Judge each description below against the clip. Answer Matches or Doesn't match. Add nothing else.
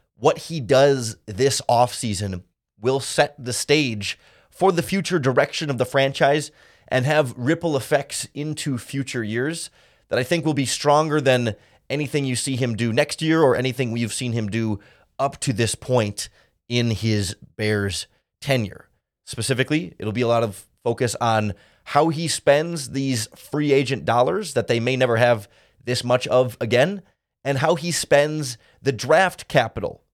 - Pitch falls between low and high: Doesn't match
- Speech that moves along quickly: Doesn't match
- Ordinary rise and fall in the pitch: Matches